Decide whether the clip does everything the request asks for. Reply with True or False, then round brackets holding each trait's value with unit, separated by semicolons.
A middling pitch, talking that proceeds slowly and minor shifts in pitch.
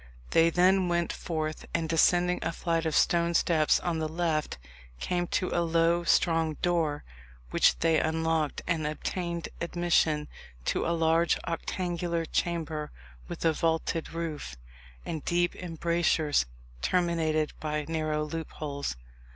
True (165 Hz; 130 wpm; 1.6 semitones)